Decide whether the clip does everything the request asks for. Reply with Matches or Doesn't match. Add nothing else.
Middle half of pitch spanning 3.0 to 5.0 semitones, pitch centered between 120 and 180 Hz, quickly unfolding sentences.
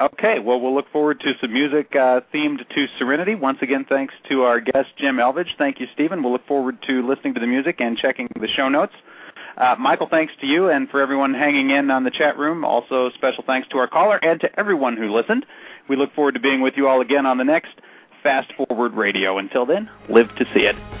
Doesn't match